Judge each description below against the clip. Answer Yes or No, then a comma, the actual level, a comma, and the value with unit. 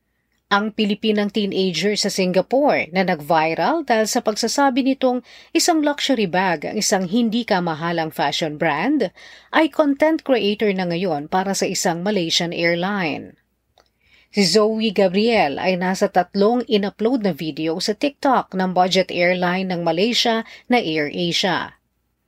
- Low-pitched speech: No, high, 200 Hz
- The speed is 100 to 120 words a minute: No, average, 130 wpm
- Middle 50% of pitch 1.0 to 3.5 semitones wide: No, average, 4.2 semitones